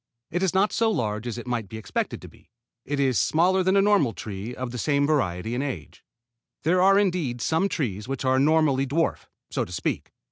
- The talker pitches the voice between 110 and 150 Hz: Yes, medium, 140 Hz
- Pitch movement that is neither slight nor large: No, wide, 6.8 semitones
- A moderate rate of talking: No, fast, 215 wpm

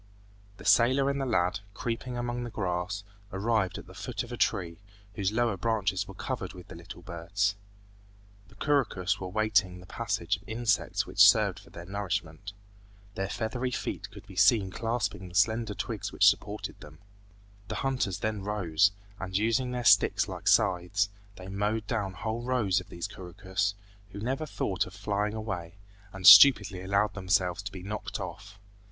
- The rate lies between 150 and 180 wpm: Yes, average, 170 wpm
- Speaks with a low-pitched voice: Yes, low, 100 Hz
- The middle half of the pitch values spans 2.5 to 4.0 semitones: Yes, average, 3.1 semitones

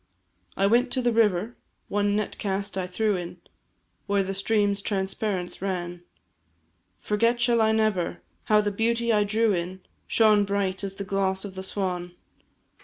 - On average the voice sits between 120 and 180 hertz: No, high, 200 Hz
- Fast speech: No, average, 160 wpm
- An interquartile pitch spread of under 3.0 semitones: Yes, narrow, 2.4 semitones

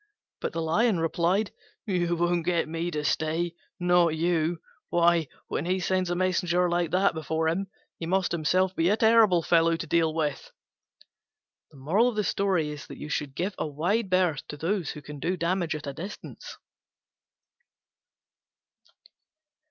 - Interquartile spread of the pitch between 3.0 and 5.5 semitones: No, narrow, 2.5 semitones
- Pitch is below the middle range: No, medium, 170 Hz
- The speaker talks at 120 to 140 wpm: Yes, slow, 135 wpm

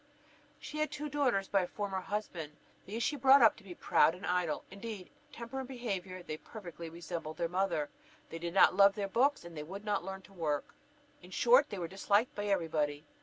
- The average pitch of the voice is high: Yes, high, 195 Hz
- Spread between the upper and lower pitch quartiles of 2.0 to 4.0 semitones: No, average, 4.7 semitones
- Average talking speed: No, fast, 215 wpm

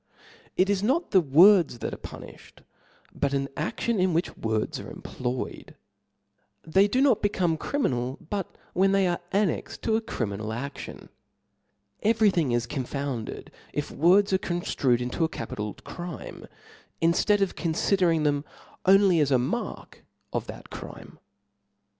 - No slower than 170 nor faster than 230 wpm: No, average, 155 wpm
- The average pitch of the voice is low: No, medium, 170 Hz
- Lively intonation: Yes, wide, 6.4 semitones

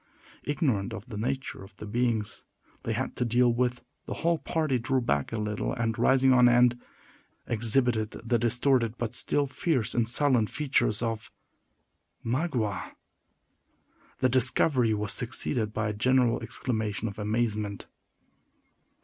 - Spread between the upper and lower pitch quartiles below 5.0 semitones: Yes, average, 3.0 semitones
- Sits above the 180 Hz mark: No, low, 120 Hz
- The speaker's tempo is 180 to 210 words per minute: No, average, 140 wpm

